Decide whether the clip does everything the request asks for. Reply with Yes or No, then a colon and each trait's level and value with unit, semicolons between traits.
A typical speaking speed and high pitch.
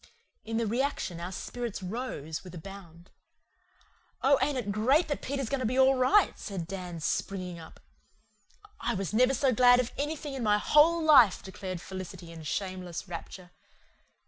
Yes: average, 170 wpm; high, 210 Hz